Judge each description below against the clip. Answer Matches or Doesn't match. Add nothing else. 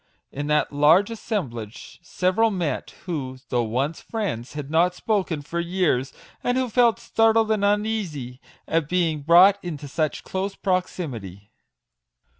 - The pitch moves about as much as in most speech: Doesn't match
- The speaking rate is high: Doesn't match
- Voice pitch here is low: Doesn't match